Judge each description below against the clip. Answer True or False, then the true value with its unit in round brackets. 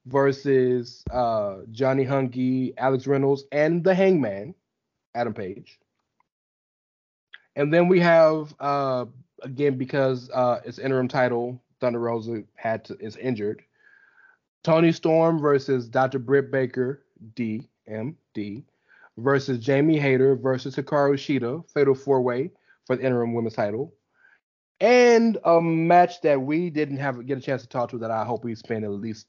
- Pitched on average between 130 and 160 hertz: True (135 Hz)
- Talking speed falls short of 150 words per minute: True (135 wpm)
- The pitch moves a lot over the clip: False (3.1 semitones)